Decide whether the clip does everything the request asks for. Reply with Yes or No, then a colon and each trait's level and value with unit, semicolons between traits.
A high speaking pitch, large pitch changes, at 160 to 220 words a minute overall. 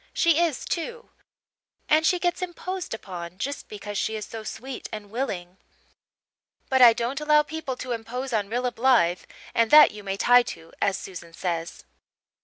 Yes: high, 240 Hz; wide, 7.0 semitones; average, 170 wpm